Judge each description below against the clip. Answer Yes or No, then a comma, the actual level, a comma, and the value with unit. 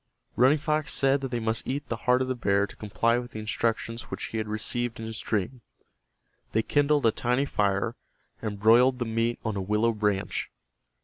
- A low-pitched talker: Yes, low, 115 Hz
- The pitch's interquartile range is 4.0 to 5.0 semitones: No, average, 2.8 semitones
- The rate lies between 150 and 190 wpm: No, average, 200 wpm